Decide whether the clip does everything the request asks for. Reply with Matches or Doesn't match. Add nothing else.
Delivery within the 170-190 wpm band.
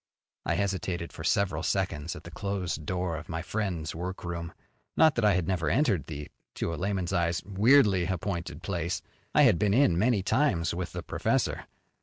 Matches